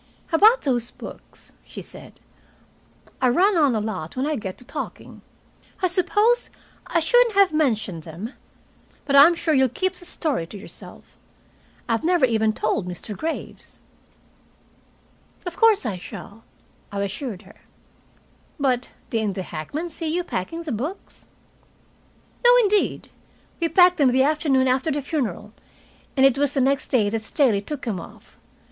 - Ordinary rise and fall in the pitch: No, wide, 7.4 semitones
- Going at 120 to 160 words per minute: Yes, average, 155 wpm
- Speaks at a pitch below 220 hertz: No, very high, 270 Hz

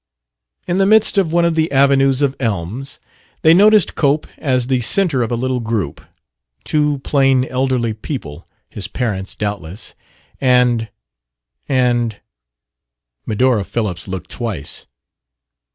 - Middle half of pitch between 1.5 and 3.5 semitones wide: No, average, 4.4 semitones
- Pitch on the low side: Yes, low, 125 Hz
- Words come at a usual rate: No, slow, 125 wpm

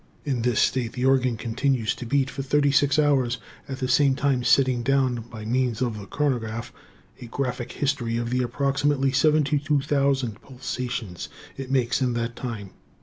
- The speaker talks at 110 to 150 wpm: No, average, 165 wpm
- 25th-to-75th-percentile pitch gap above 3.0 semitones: No, narrow, 2.6 semitones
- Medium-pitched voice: No, low, 130 Hz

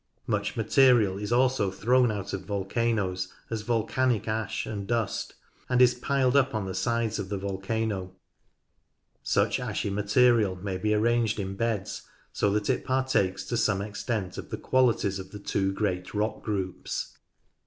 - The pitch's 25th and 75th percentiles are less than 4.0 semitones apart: Yes, average, 3.3 semitones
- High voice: No, low, 105 Hz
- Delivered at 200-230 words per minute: No, average, 160 wpm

